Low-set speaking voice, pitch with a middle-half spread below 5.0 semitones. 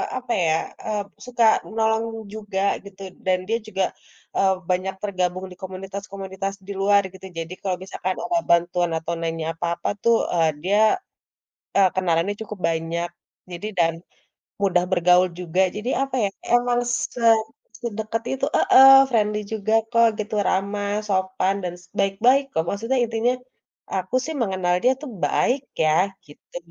No: high, 195 Hz; average, 3.6 semitones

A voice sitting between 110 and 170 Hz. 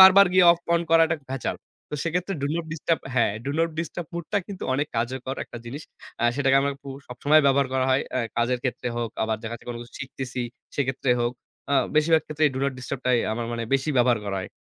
Yes: low, 135 Hz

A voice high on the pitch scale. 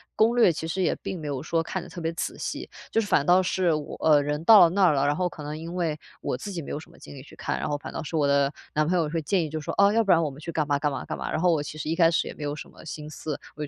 No: medium, 160 Hz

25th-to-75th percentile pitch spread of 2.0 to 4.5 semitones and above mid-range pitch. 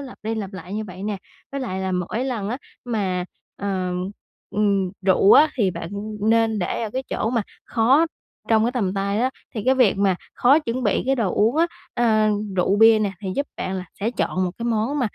Yes: average, 3.9 semitones; high, 215 Hz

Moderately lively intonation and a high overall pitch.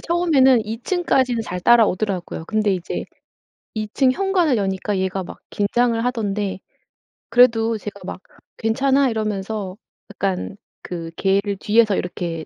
Yes: average, 4.2 semitones; high, 215 Hz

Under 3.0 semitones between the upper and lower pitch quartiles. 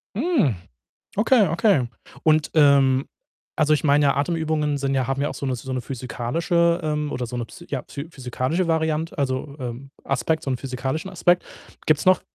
No: average, 3.7 semitones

